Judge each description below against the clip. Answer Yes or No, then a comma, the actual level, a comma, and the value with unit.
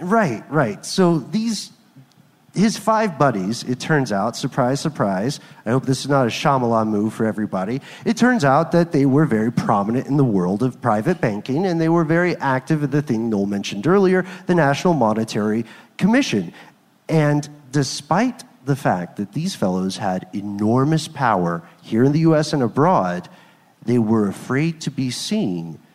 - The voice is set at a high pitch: No, medium, 140 Hz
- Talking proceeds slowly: No, average, 170 wpm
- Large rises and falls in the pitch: Yes, wide, 6.8 semitones